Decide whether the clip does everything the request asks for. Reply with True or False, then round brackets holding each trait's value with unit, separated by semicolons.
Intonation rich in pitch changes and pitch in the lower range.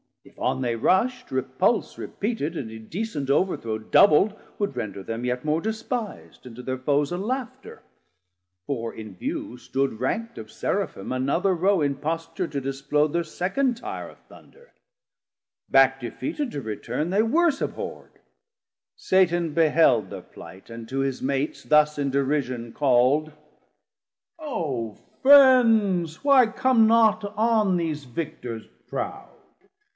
False (8.6 semitones; 150 Hz)